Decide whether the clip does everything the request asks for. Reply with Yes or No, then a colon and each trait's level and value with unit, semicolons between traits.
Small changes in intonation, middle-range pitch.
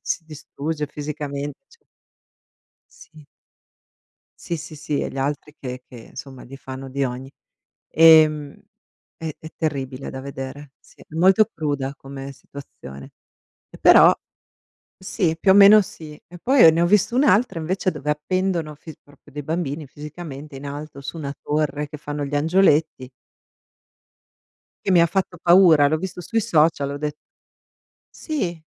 No: average, 3.4 semitones; medium, 150 Hz